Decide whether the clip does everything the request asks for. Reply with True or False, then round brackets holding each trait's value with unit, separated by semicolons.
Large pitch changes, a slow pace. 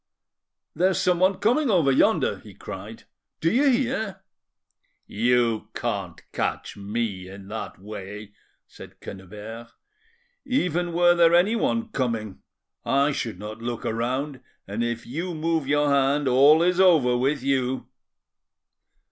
True (8.0 semitones; 125 wpm)